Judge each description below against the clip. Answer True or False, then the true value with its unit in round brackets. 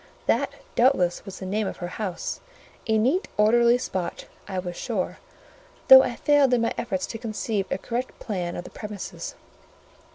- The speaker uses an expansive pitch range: False (4.3 semitones)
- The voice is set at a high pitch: True (215 Hz)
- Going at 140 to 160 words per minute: False (170 wpm)